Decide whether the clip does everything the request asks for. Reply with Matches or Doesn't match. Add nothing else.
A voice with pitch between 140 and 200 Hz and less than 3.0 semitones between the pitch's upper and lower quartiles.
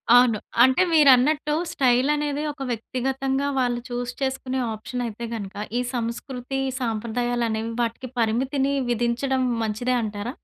Doesn't match